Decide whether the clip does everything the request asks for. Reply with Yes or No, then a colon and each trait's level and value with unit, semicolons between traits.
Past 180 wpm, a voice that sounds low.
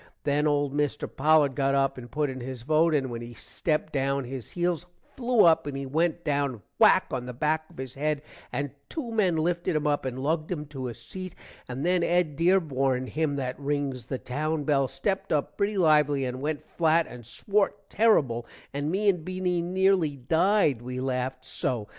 No: average, 195 wpm; medium, 145 Hz